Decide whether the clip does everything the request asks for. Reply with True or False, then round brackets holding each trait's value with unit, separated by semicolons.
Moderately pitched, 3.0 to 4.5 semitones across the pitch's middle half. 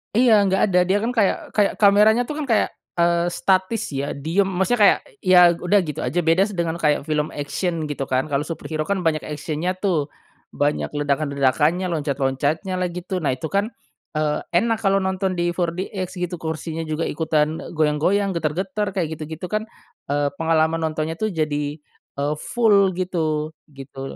True (170 Hz; 4.0 semitones)